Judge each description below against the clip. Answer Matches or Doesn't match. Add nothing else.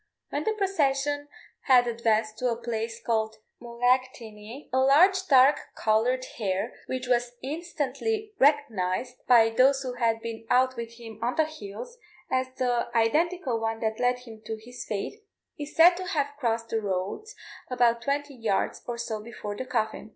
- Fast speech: Doesn't match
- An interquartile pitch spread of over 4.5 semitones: Doesn't match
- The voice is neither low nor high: Doesn't match